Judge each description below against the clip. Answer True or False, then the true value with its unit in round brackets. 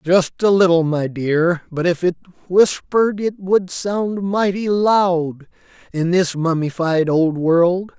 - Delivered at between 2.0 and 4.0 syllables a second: True (3.6 syllables/s)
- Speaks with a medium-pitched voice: True (180 Hz)